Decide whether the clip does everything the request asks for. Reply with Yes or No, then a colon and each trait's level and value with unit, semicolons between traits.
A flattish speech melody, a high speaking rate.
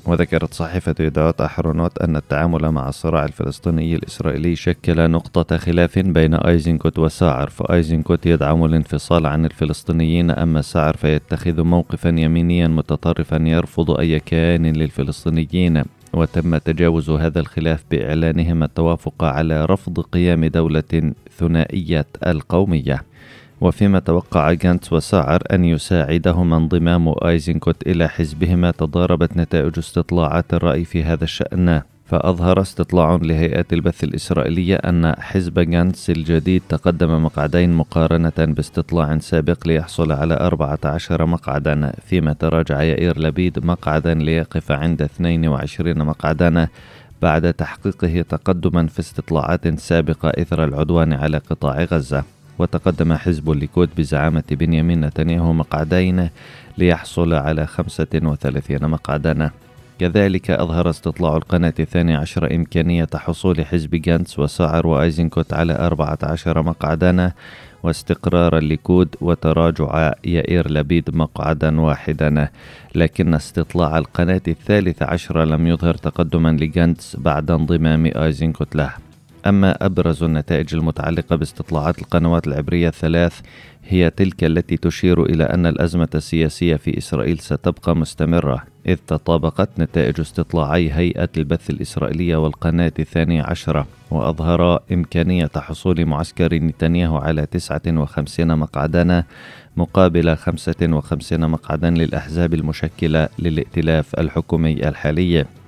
No: narrow, 1.6 semitones; average, 110 wpm